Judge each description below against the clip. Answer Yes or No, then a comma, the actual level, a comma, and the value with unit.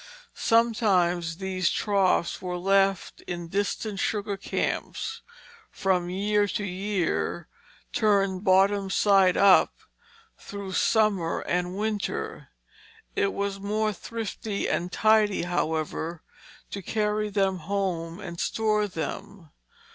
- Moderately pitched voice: No, high, 195 Hz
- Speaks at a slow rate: Yes, slow, 110 wpm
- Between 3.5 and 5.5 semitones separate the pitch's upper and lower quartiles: No, narrow, 2.5 semitones